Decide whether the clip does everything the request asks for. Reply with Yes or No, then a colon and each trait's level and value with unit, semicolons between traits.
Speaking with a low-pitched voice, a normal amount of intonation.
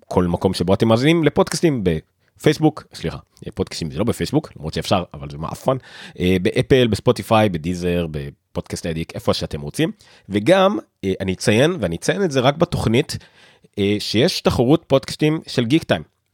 No: low, 105 Hz; wide, 7.4 semitones